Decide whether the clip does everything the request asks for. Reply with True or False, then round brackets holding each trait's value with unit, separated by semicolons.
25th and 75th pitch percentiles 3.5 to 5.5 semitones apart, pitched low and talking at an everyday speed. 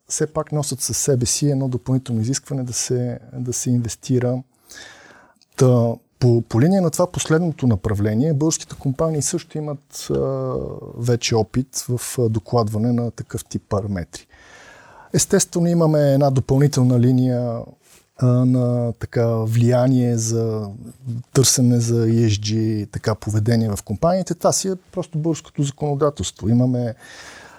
True (3.9 semitones; 125 Hz; 130 wpm)